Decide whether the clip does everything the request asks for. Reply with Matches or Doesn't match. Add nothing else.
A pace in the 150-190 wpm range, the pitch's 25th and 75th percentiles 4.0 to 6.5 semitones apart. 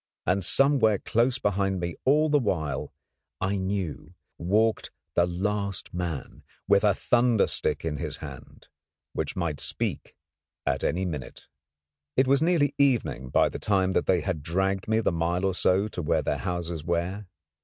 Matches